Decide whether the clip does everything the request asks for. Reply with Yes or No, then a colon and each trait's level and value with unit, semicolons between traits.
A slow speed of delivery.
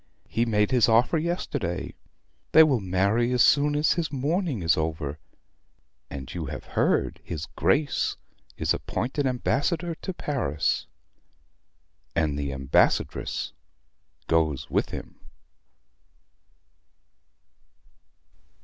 Yes: slow, 105 wpm